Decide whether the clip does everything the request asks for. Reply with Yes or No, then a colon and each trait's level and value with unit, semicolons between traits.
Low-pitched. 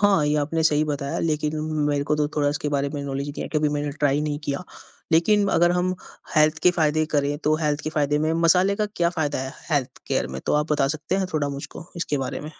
No: medium, 150 Hz